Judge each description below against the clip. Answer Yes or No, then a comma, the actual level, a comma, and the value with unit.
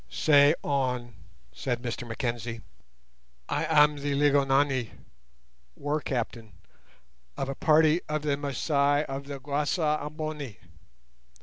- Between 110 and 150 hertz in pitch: Yes, medium, 140 Hz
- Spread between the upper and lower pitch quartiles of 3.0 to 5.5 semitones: No, narrow, 2.6 semitones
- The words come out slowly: Yes, slow, 110 wpm